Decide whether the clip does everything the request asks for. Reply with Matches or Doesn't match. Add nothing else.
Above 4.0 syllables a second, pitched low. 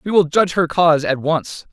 Doesn't match